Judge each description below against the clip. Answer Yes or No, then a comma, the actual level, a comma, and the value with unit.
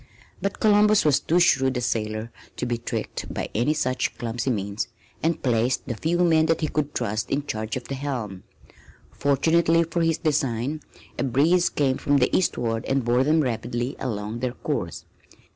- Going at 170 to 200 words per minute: Yes, average, 175 wpm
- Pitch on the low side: Yes, low, 130 Hz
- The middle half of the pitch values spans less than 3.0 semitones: No, average, 5.1 semitones